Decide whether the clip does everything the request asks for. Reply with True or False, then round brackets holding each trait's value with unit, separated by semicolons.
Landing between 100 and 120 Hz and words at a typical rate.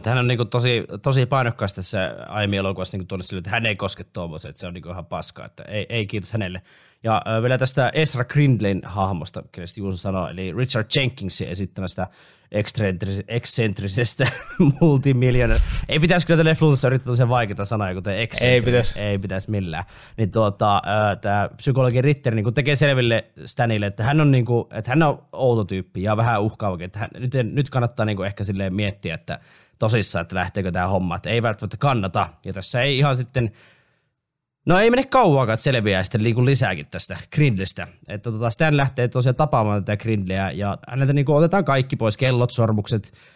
False (110 Hz; 160 wpm)